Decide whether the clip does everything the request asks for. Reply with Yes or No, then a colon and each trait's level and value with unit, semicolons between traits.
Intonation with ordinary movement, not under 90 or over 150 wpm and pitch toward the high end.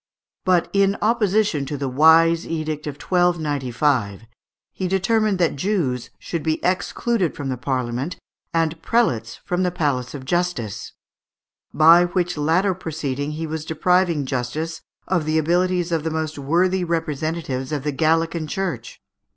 No: average, 3.8 semitones; average, 140 wpm; medium, 160 Hz